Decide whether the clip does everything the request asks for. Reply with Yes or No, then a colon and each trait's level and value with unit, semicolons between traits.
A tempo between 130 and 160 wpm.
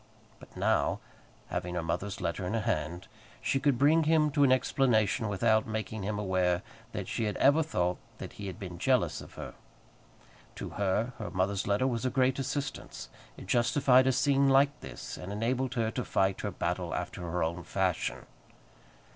No: average, 180 wpm